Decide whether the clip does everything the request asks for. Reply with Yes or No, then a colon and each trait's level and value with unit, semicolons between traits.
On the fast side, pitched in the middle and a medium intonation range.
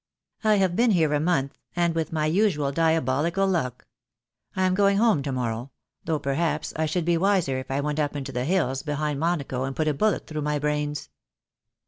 Yes: fast, 215 wpm; medium, 155 Hz; average, 4.0 semitones